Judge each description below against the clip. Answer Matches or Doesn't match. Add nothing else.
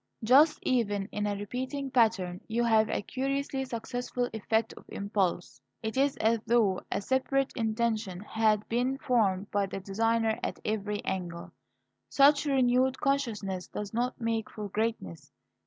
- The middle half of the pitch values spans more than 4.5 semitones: Doesn't match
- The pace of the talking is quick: Doesn't match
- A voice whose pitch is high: Matches